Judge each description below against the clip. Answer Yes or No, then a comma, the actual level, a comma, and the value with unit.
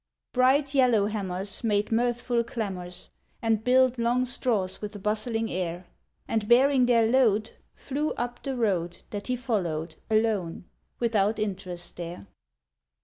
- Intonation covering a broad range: No, average, 4.0 semitones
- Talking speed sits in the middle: No, slow, 130 wpm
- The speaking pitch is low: No, high, 220 Hz